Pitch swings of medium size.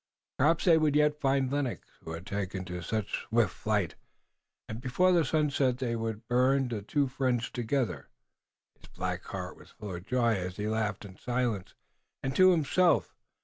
Yes: average, 5.0 semitones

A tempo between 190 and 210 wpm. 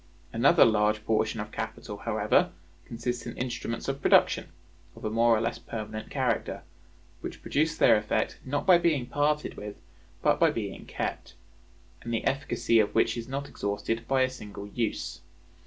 No: average, 165 wpm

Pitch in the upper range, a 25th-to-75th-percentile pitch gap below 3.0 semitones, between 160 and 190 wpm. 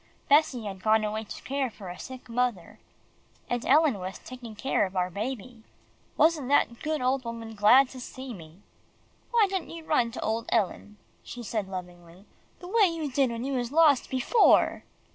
No: high, 240 Hz; average, 4.6 semitones; average, 180 wpm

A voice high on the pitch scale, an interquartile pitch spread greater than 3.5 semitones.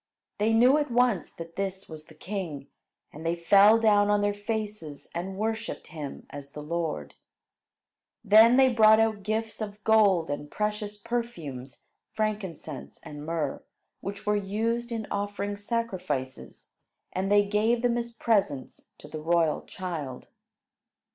Yes: high, 205 Hz; average, 5.0 semitones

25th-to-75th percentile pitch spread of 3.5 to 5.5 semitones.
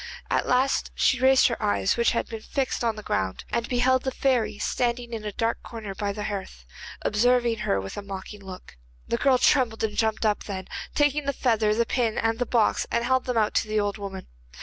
No: average, 3.1 semitones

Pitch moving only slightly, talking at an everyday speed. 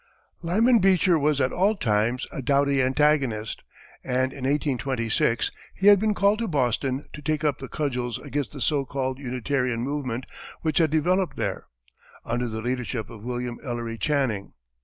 No: average, 3.8 semitones; average, 160 wpm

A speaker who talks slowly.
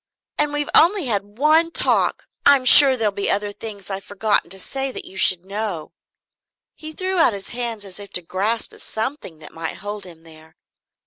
No: average, 200 wpm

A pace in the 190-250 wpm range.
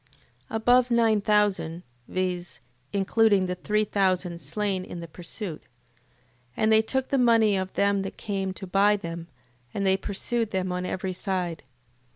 No: average, 160 wpm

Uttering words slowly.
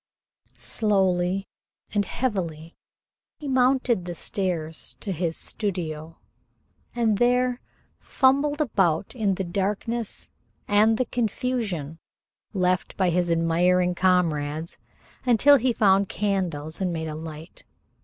Yes: slow, 110 wpm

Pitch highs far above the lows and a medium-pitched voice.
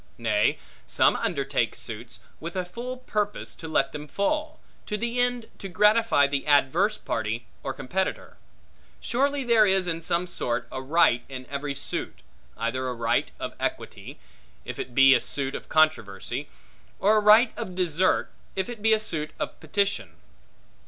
Yes: wide, 7.9 semitones; medium, 175 Hz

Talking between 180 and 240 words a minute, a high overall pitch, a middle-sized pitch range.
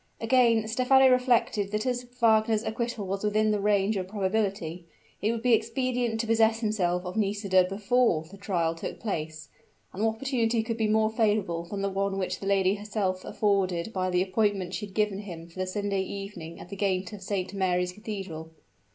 Yes: average, 190 wpm; high, 205 Hz; average, 3.0 semitones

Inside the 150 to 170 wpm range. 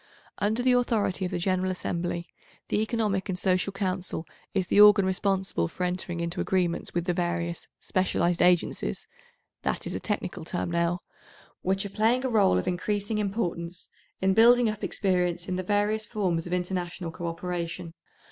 Yes: average, 160 wpm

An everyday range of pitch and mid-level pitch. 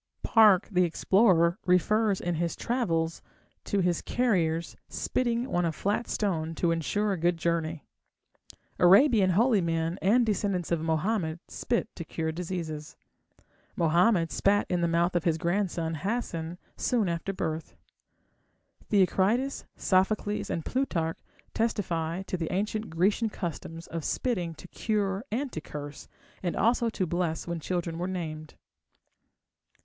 Yes: average, 3.9 semitones; medium, 180 Hz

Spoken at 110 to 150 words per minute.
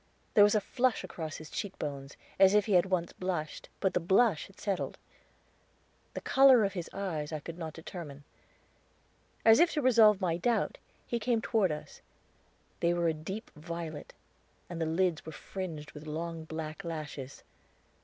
No: average, 175 wpm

